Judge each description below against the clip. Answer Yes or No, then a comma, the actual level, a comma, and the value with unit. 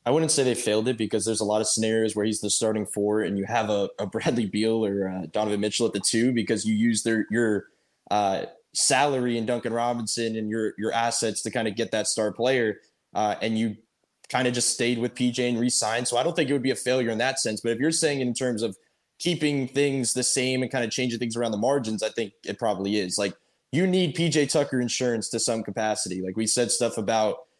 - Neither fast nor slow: No, fast, 245 wpm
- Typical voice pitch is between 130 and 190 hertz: No, low, 115 Hz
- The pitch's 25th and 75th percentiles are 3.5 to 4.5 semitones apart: No, narrow, 2.6 semitones